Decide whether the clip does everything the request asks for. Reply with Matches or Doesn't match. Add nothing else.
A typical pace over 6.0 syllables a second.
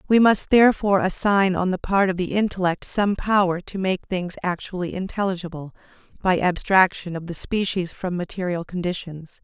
Doesn't match